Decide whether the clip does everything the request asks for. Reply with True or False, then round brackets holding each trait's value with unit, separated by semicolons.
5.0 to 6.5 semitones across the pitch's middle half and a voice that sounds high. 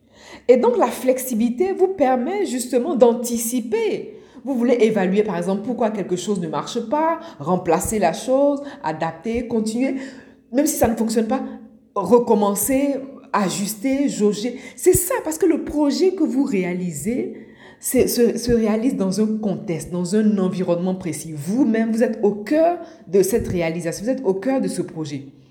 True (5.5 semitones; 235 Hz)